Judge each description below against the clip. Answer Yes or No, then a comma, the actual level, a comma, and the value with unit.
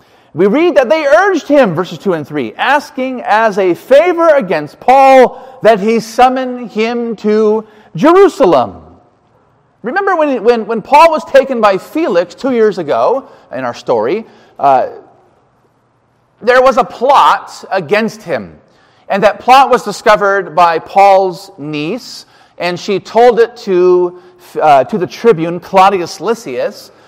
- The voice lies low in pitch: No, high, 220 Hz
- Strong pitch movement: Yes, wide, 6.6 semitones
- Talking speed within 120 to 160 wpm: Yes, average, 140 wpm